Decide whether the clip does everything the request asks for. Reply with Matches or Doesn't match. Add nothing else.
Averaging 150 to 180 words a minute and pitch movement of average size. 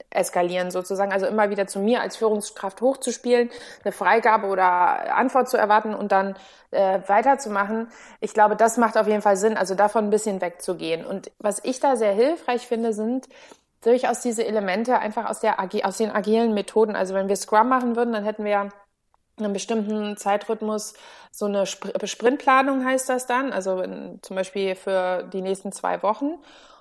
Matches